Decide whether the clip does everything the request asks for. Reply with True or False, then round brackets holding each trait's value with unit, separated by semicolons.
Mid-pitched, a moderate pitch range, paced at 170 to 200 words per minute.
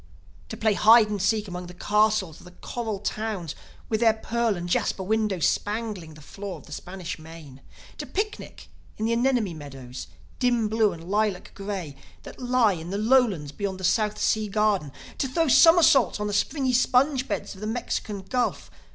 False (210 Hz; 4.2 semitones; 185 wpm)